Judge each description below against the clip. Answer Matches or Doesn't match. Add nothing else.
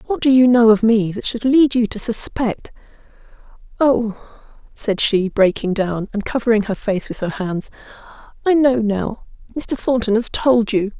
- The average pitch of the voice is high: Matches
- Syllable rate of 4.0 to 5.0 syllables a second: Matches